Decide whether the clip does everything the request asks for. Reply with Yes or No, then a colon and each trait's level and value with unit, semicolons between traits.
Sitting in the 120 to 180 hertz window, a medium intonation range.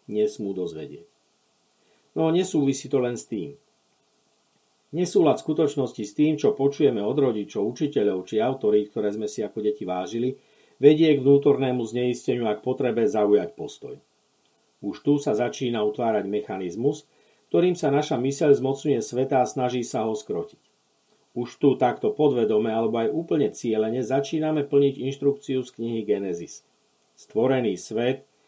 Yes: low, 130 Hz; average, 4.3 semitones